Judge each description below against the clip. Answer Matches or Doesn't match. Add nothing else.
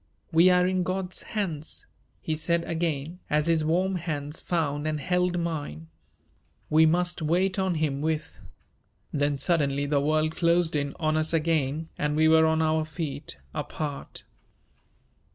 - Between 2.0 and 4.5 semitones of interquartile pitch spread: Matches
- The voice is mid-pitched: Matches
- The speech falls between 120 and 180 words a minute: Matches